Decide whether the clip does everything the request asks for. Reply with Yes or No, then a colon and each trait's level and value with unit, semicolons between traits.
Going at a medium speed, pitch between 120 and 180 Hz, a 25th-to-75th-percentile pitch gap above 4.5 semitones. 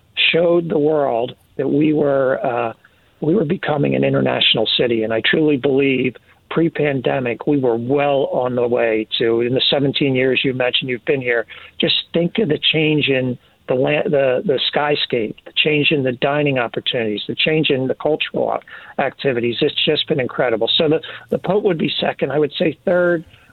No: average, 185 wpm; low, 135 Hz; average, 4.1 semitones